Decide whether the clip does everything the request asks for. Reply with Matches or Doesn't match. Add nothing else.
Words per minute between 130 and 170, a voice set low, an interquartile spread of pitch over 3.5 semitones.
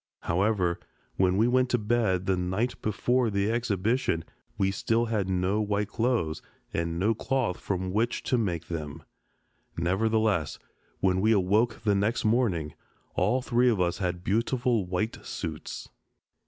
Matches